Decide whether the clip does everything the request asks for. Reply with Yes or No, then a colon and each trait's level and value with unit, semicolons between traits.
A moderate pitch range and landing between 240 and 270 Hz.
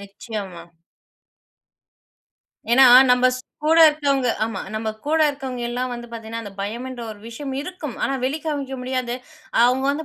Yes: average, 3.5 semitones; very high, 250 Hz